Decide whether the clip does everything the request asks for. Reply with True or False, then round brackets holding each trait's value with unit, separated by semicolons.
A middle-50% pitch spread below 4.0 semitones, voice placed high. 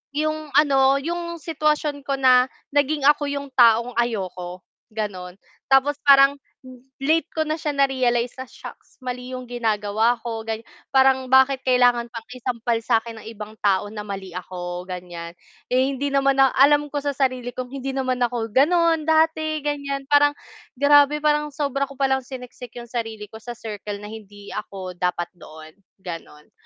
False (4.3 semitones; 255 Hz)